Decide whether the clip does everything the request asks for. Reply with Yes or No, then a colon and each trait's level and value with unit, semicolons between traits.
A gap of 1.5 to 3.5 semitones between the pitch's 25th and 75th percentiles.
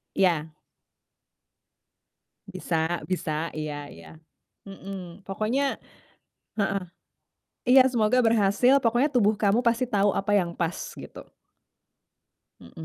No: average, 5.3 semitones